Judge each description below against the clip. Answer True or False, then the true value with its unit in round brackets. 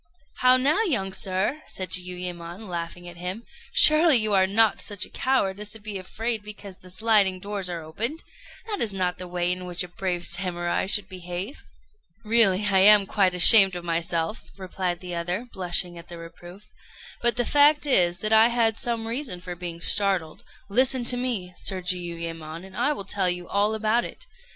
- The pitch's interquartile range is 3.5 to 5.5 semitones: True (4.0 semitones)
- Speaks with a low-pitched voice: False (190 Hz)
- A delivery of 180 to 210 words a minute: True (190 wpm)